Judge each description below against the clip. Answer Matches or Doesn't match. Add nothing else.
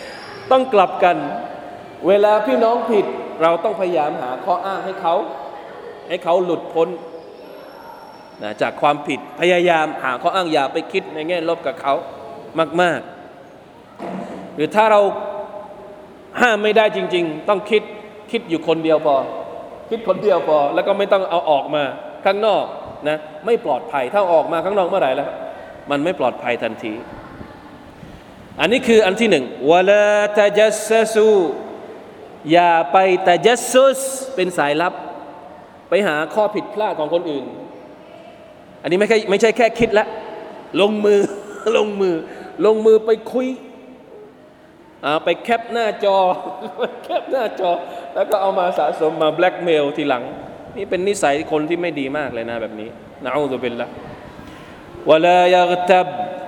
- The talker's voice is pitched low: Doesn't match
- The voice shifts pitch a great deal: Doesn't match